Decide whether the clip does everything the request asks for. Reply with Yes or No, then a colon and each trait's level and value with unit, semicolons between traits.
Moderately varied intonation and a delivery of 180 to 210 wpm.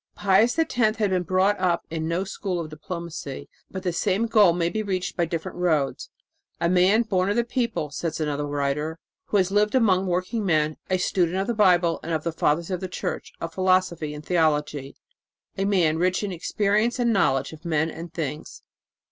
Yes: average, 3.7 semitones; average, 200 wpm